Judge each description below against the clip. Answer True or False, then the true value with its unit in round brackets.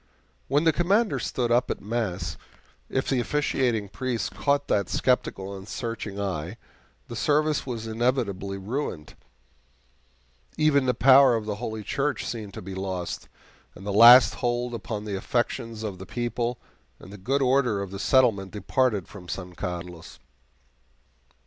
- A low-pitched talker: True (115 Hz)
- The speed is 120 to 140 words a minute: False (150 wpm)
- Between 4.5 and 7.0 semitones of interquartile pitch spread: True (4.8 semitones)